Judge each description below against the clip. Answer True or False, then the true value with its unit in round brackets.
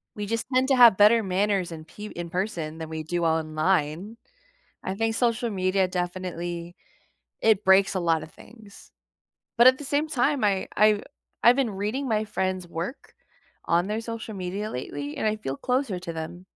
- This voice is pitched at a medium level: False (195 Hz)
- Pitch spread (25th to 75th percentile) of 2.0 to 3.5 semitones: False (4.4 semitones)